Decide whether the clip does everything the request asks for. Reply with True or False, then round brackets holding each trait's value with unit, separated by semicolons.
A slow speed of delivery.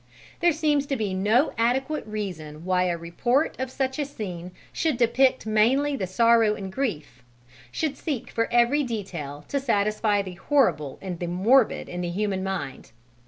False (165 wpm)